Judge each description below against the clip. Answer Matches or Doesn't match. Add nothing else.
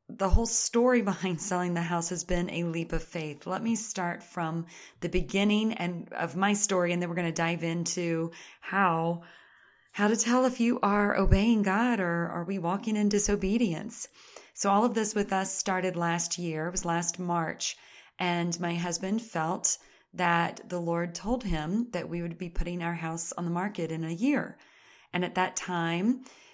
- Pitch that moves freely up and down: Doesn't match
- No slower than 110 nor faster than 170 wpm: Doesn't match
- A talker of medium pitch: Matches